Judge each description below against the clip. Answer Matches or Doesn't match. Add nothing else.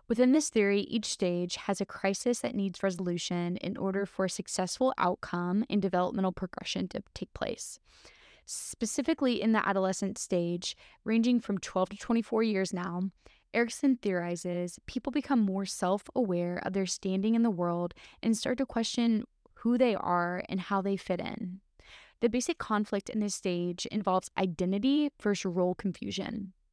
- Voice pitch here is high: Matches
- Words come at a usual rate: Matches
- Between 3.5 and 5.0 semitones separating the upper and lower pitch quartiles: Matches